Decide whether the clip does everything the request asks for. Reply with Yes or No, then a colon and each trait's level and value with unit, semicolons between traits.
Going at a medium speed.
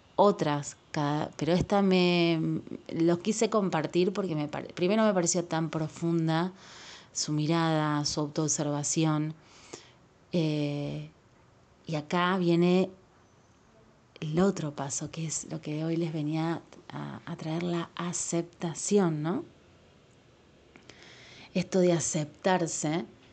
No: slow, 105 wpm